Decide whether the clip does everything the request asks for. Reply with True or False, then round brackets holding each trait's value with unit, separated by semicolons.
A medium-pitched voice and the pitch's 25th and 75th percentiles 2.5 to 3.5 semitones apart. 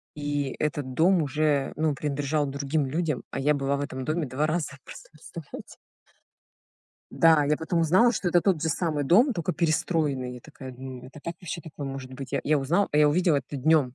True (150 Hz; 2.9 semitones)